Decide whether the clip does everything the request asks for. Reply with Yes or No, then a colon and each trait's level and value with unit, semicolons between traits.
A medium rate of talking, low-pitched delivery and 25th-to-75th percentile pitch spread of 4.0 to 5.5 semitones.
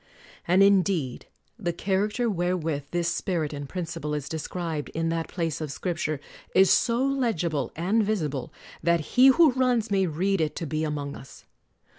No: average, 165 wpm; medium, 170 Hz; average, 4.3 semitones